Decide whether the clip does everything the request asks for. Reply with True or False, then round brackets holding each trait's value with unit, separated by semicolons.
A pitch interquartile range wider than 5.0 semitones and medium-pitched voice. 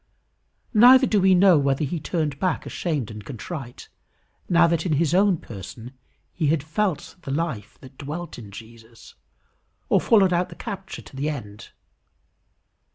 True (5.6 semitones; 155 Hz)